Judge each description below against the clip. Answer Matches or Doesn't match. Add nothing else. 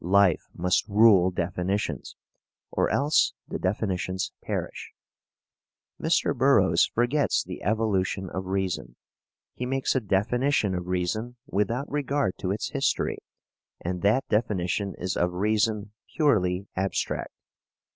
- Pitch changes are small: Doesn't match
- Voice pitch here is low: Matches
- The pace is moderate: Doesn't match